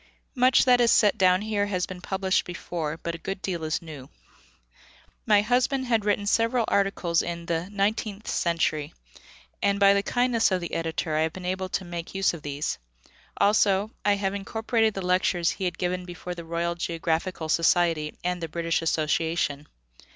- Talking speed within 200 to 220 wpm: No, average, 180 wpm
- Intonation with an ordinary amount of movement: Yes, average, 3.3 semitones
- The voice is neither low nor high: Yes, medium, 180 Hz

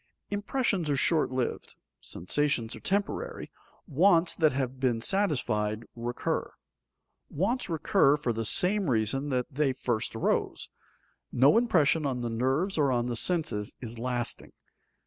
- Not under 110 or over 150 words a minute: Yes, average, 140 wpm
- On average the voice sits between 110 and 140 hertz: Yes, low, 135 Hz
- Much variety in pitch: Yes, wide, 6.1 semitones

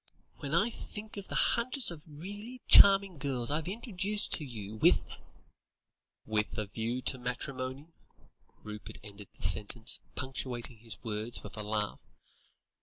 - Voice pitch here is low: Yes, low, 130 Hz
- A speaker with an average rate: Yes, average, 145 wpm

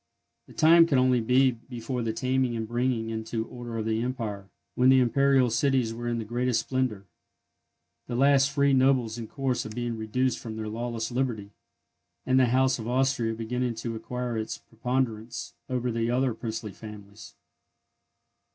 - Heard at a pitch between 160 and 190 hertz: No, low, 120 Hz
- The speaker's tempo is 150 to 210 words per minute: Yes, average, 170 wpm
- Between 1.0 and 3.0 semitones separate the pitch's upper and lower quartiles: Yes, narrow, 2.4 semitones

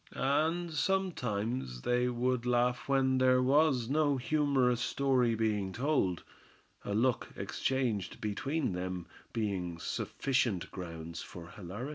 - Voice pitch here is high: No, low, 125 Hz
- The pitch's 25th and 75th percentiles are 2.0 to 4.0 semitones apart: No, average, 5.2 semitones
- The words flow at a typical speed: No, slow, 115 wpm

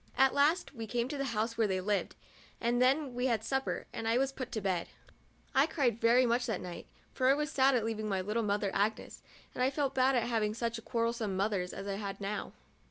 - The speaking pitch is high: Yes, high, 235 Hz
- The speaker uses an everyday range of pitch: Yes, average, 3.7 semitones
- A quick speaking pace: Yes, fast, 235 wpm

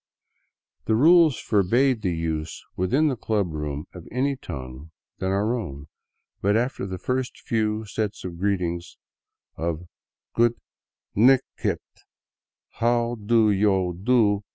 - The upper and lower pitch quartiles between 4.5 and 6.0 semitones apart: Yes, average, 5.1 semitones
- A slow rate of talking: Yes, slow, 130 wpm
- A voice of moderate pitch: No, low, 105 Hz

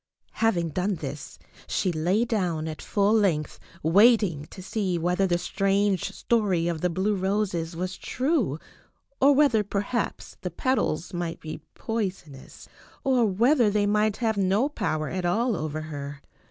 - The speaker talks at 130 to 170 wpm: Yes, average, 150 wpm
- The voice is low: No, high, 190 Hz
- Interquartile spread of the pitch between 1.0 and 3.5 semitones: No, average, 4.5 semitones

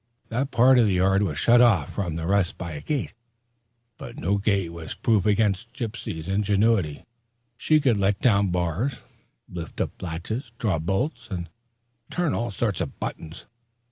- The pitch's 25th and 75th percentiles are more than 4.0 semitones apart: Yes, average, 5.0 semitones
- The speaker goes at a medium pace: Yes, average, 165 wpm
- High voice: No, low, 100 Hz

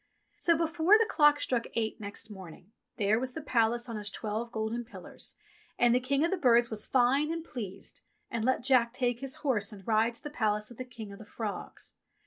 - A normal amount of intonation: Yes, average, 3.5 semitones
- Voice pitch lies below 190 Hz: No, high, 235 Hz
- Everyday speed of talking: No, fast, 215 wpm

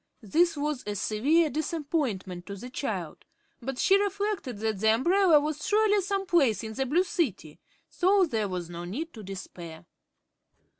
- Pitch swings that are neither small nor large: No, wide, 9.0 semitones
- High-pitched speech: Yes, very high, 270 Hz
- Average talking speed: Yes, average, 160 wpm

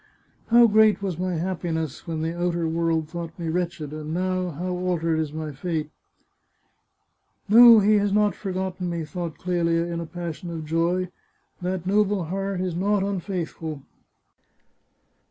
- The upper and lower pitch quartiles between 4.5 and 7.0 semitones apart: No, narrow, 2.5 semitones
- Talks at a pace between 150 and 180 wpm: Yes, average, 170 wpm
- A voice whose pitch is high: No, medium, 175 Hz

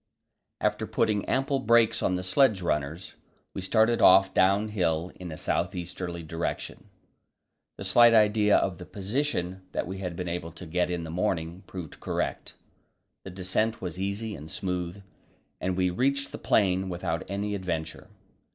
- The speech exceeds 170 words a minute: No, average, 160 wpm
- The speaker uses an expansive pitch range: No, average, 3.1 semitones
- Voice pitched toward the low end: Yes, very low, 95 Hz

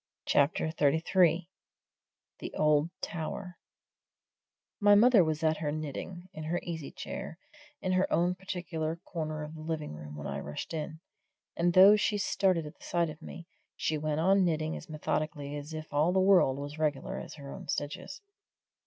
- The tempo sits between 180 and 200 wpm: No, average, 170 wpm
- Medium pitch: Yes, medium, 160 Hz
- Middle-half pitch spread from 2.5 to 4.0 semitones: Yes, average, 2.8 semitones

